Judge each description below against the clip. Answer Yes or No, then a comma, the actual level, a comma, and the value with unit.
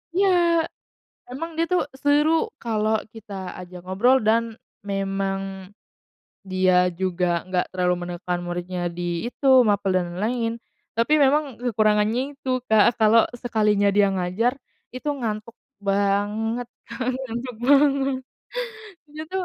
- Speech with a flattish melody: No, average, 4.5 semitones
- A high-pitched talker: Yes, high, 215 Hz